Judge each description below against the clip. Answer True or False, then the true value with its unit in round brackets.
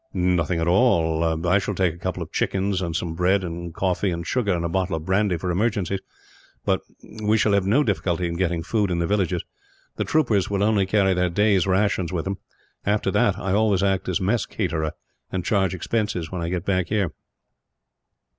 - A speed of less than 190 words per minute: False (200 wpm)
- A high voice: False (95 Hz)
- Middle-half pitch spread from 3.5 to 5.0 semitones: False (2.8 semitones)